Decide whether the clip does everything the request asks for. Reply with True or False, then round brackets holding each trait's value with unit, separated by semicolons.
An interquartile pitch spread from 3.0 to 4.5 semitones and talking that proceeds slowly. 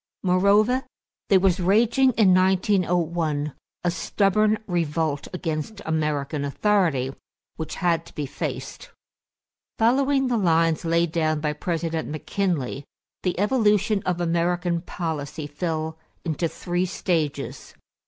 True (3.8 semitones; 115 wpm)